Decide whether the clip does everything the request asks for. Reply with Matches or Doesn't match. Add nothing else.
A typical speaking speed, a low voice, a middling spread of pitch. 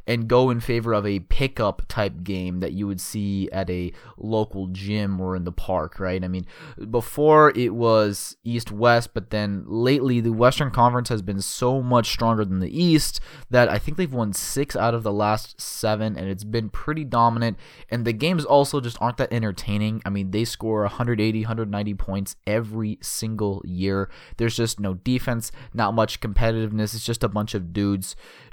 Matches